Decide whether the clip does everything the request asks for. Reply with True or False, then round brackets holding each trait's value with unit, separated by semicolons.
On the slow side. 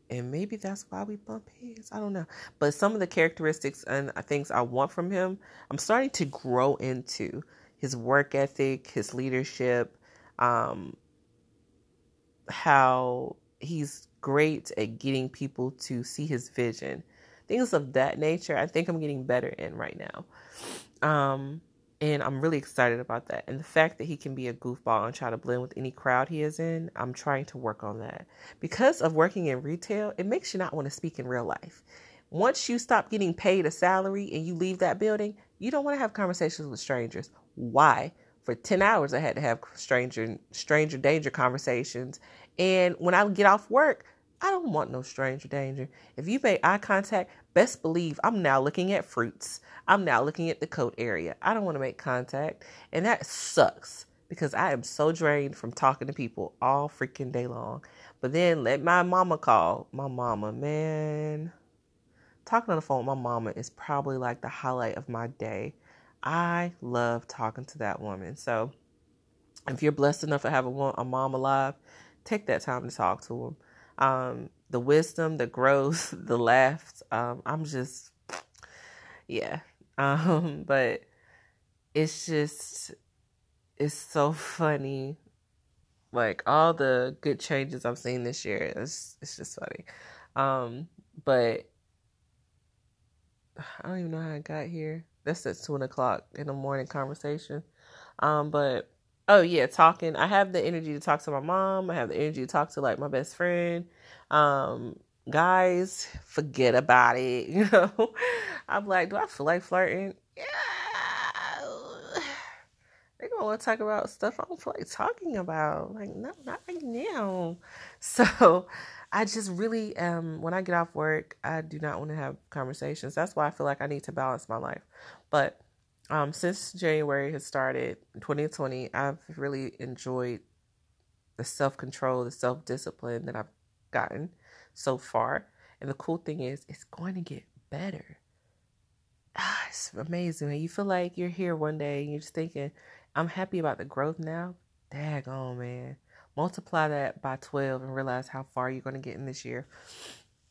False (175 wpm)